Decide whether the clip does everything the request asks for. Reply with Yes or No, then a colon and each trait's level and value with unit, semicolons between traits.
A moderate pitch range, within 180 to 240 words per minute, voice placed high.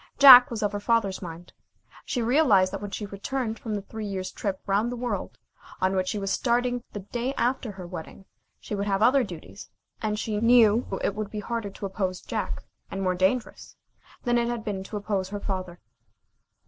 Yes: average, 3.4 semitones; average, 200 wpm; high, 210 Hz